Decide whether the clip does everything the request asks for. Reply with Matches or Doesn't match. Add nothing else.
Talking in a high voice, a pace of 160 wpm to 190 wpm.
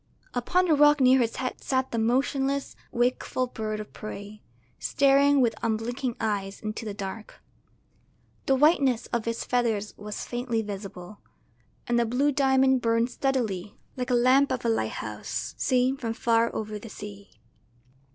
Doesn't match